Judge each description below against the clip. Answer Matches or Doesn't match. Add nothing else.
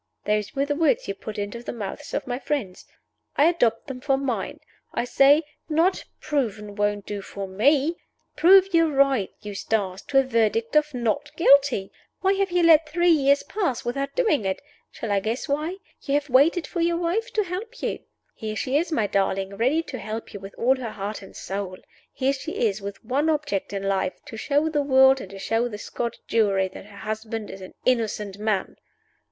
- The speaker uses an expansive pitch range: Matches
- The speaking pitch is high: Matches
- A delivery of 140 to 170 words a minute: Doesn't match